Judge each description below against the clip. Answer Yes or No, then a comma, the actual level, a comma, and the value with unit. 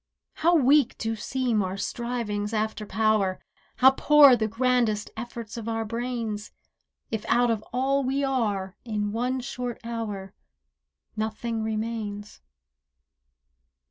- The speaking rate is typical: No, slow, 120 wpm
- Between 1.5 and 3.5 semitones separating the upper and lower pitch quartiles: Yes, average, 2.7 semitones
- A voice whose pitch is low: No, high, 225 Hz